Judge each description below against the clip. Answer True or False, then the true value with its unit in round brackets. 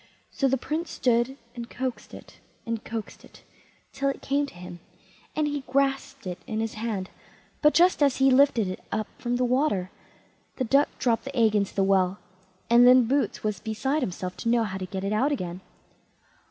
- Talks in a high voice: True (235 Hz)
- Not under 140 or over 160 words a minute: False (195 wpm)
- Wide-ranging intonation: False (4.9 semitones)